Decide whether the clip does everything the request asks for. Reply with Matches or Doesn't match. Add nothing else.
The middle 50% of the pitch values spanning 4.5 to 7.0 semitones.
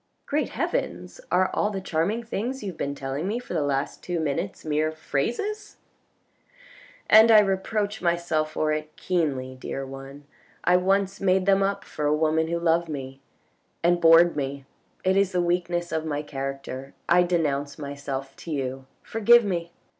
Matches